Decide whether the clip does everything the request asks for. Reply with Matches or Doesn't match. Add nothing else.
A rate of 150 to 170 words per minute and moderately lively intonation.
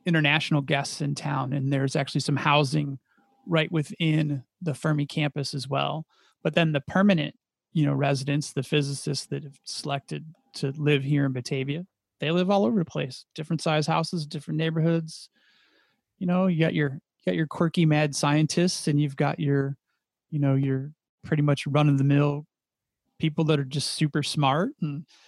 Doesn't match